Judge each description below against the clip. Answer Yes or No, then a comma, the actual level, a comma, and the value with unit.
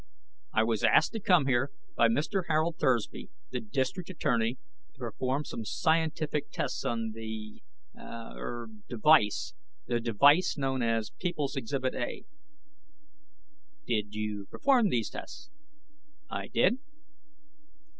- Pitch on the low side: Yes, low, 130 Hz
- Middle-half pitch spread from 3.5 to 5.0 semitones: No, wide, 5.6 semitones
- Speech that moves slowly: Yes, slow, 120 wpm